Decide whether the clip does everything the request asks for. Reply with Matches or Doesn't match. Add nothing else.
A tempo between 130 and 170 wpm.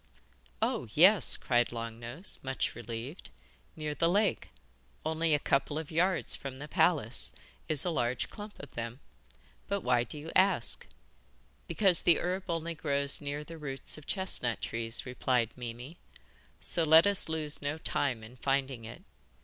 Matches